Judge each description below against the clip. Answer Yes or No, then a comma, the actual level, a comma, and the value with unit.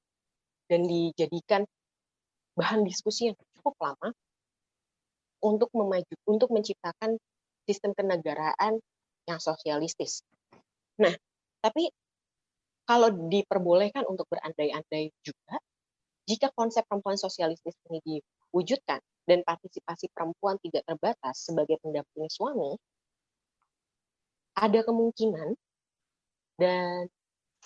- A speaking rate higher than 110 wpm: No, slow, 85 wpm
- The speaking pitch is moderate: Yes, medium, 180 Hz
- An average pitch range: Yes, average, 5.0 semitones